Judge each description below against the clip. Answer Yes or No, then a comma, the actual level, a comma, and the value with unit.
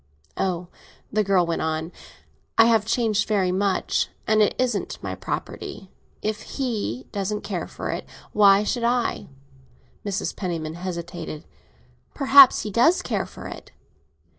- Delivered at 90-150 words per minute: Yes, average, 140 wpm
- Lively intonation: No, average, 3.7 semitones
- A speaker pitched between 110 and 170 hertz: No, high, 205 Hz